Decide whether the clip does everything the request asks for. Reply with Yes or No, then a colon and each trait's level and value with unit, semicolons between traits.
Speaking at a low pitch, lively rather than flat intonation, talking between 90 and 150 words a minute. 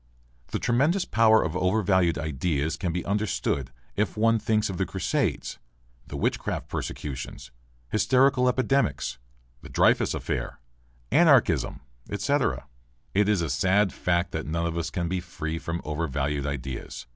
Yes: very low, 90 Hz; wide, 5.9 semitones; average, 140 wpm